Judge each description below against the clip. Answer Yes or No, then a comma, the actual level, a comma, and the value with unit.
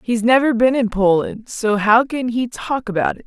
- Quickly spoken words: Yes, fast, 220 wpm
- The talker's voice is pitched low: No, high, 235 Hz